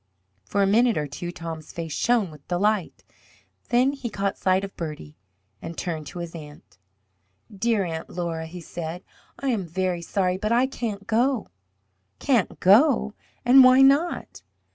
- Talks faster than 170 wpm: No, average, 160 wpm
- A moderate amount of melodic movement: No, wide, 6.0 semitones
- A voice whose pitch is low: No, high, 190 Hz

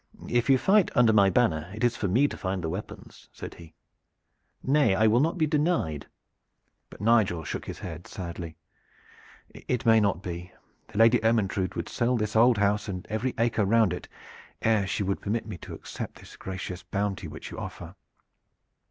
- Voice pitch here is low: Yes, low, 105 Hz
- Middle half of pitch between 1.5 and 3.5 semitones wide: No, average, 4.1 semitones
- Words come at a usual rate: Yes, average, 185 wpm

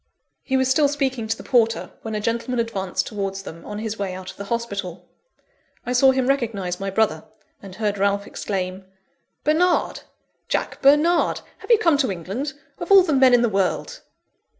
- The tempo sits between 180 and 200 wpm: Yes, average, 185 wpm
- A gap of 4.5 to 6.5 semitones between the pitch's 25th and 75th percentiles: Yes, average, 5.2 semitones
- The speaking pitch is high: Yes, high, 225 Hz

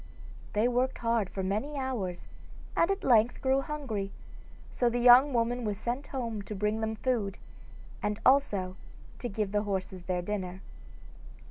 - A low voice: No, high, 220 Hz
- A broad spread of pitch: No, average, 4.2 semitones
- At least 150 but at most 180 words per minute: Yes, average, 155 wpm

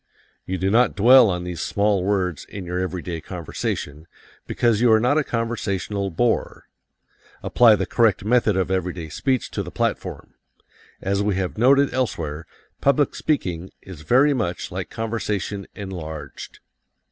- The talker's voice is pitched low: Yes, low, 100 Hz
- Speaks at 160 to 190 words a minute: No, average, 145 wpm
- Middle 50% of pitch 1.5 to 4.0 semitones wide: No, average, 4.6 semitones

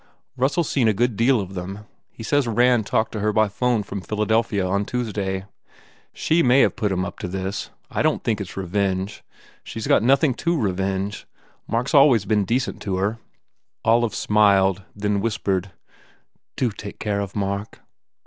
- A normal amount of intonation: Yes, average, 3.3 semitones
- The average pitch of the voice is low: Yes, low, 105 Hz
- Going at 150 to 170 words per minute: No, average, 195 wpm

